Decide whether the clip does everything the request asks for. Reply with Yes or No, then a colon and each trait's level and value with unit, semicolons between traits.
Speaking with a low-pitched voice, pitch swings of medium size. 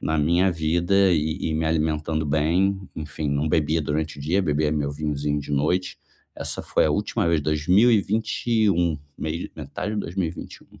Yes: very low, 80 Hz; average, 3.2 semitones